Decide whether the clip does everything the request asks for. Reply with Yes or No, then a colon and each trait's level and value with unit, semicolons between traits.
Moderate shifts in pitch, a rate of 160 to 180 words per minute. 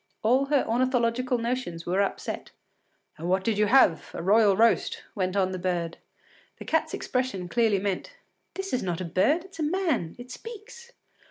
No: wide, 6.1 semitones; average, 175 wpm